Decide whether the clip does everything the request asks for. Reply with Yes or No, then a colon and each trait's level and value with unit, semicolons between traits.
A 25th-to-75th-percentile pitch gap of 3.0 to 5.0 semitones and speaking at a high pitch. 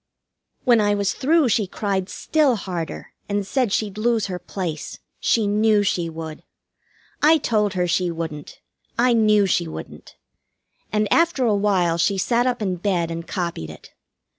Yes: average, 4.2 semitones; high, 205 Hz